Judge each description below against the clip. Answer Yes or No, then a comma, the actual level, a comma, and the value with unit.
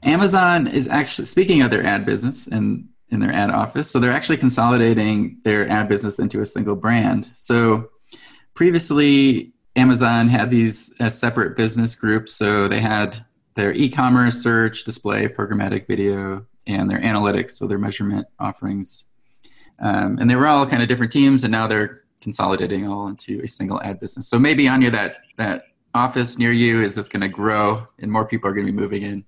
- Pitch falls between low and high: No, low, 115 Hz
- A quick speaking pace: No, average, 185 wpm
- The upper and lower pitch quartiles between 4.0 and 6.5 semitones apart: No, average, 3.3 semitones